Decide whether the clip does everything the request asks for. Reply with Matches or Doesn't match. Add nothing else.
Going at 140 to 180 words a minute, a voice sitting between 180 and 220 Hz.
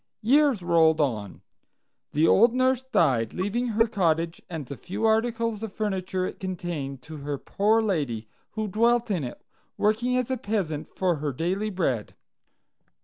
Matches